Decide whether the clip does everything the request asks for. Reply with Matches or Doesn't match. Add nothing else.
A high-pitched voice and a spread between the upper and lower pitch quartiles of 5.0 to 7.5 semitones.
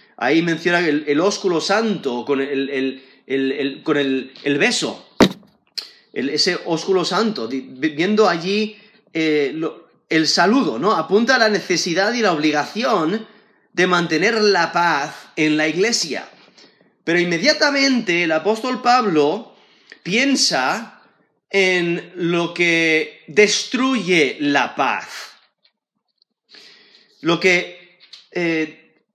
Doesn't match